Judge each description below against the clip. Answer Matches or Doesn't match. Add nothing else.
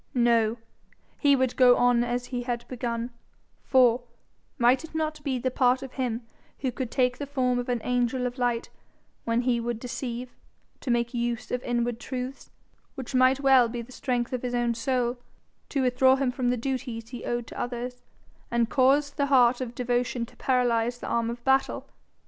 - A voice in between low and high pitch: Doesn't match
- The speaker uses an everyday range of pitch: Doesn't match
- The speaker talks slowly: Doesn't match